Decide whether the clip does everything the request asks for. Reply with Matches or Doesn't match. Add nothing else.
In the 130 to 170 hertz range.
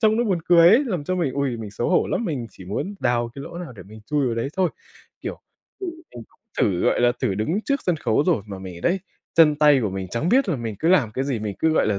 Matches